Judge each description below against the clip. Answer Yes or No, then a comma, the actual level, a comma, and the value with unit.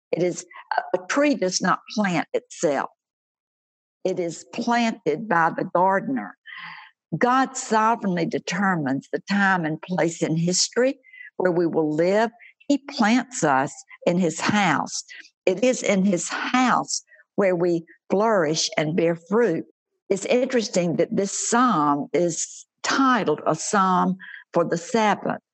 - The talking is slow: Yes, slow, 130 wpm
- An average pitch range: No, wide, 6.3 semitones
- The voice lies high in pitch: Yes, high, 195 Hz